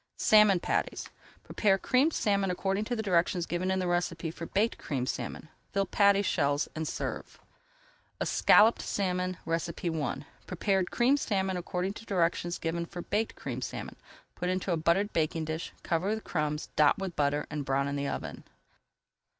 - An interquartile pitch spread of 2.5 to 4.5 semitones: Yes, average, 3.5 semitones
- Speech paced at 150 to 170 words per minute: Yes, average, 160 wpm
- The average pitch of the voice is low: No, medium, 180 Hz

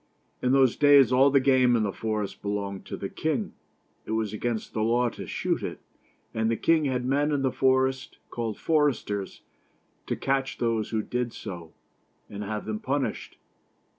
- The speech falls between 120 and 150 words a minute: No, average, 175 wpm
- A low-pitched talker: Yes, low, 120 Hz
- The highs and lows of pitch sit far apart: No, average, 3.8 semitones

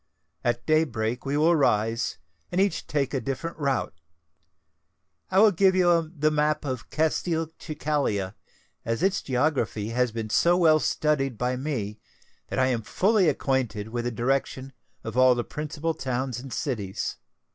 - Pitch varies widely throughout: No, average, 4.6 semitones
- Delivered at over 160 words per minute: No, average, 155 wpm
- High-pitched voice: No, low, 135 Hz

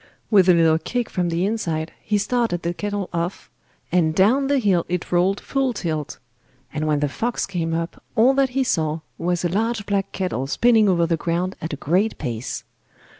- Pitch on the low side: No, medium, 180 Hz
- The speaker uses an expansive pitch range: No, average, 4.6 semitones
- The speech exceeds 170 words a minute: Yes, average, 195 wpm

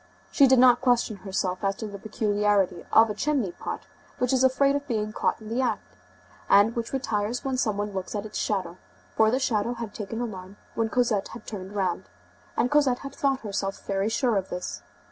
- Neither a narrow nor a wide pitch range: Yes, average, 3.8 semitones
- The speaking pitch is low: No, high, 215 Hz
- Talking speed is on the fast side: Yes, fast, 210 wpm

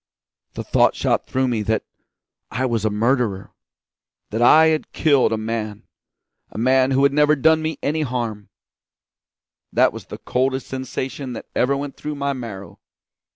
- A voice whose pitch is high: No, low, 130 Hz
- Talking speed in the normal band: Yes, average, 160 wpm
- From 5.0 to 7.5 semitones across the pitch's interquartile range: No, average, 3.8 semitones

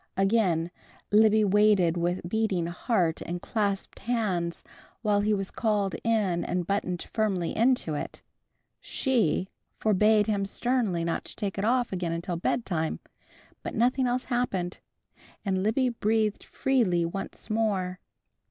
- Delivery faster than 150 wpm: No, slow, 135 wpm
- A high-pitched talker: Yes, high, 200 Hz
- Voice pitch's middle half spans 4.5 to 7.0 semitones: No, average, 3.8 semitones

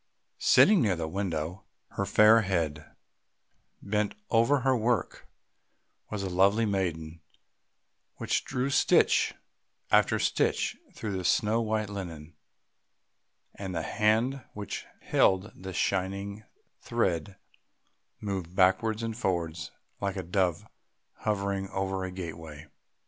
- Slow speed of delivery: Yes, slow, 115 wpm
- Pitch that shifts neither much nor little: Yes, average, 3.3 semitones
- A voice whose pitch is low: Yes, very low, 95 Hz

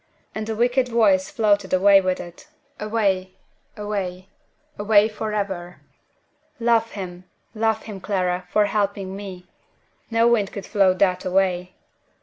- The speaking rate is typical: No, slow, 130 wpm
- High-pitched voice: Yes, high, 200 Hz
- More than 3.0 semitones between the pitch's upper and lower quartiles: No, average, 2.7 semitones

